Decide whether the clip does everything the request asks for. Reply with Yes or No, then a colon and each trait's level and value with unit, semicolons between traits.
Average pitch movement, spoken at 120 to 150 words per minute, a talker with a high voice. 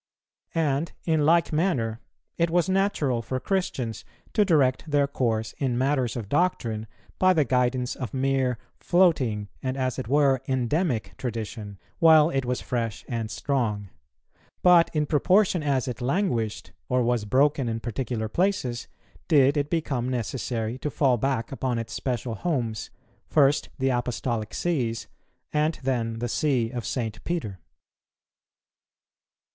No: average, 4.4 semitones; average, 140 wpm; low, 130 Hz